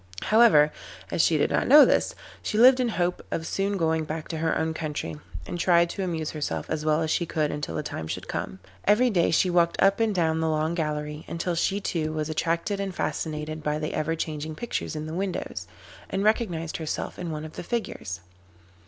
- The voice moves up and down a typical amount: Yes, average, 3.4 semitones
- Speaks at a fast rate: Yes, fast, 215 wpm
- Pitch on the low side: No, medium, 160 Hz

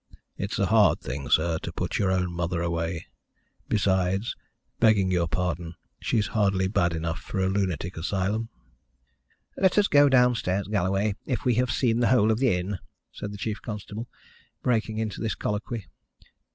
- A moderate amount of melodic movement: Yes, average, 3.7 semitones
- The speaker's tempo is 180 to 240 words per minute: No, average, 165 wpm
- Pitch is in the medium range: No, low, 100 Hz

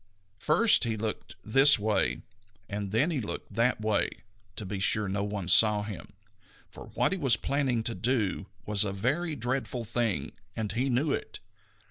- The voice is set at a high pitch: No, low, 110 Hz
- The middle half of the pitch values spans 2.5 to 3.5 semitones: No, average, 4.1 semitones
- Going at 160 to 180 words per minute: Yes, average, 175 wpm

